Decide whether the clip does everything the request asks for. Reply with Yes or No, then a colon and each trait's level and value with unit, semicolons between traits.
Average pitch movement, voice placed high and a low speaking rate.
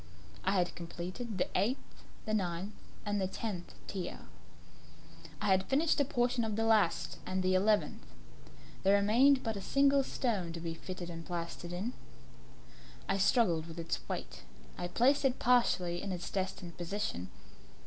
No: average, 4.7 semitones; high, 195 Hz; average, 160 wpm